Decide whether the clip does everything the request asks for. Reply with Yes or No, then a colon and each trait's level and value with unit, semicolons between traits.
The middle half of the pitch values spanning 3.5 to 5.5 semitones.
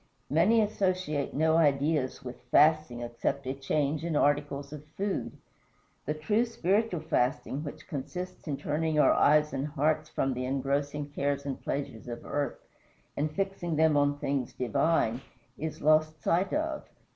No: narrow, 2.6 semitones